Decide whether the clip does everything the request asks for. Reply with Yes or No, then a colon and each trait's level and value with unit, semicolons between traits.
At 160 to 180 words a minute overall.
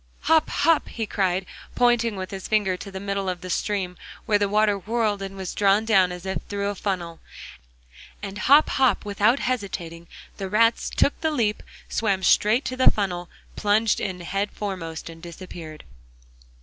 Yes: average, 175 wpm